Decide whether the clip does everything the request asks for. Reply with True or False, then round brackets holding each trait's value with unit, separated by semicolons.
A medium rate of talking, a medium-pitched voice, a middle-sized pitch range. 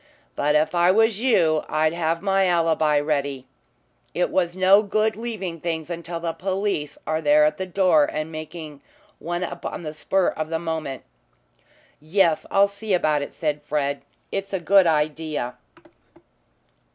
True (155 wpm; 165 Hz; 3.6 semitones)